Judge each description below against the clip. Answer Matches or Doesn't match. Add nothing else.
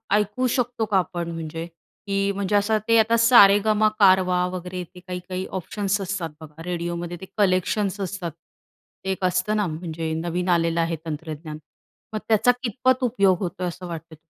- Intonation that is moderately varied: Matches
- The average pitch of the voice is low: Doesn't match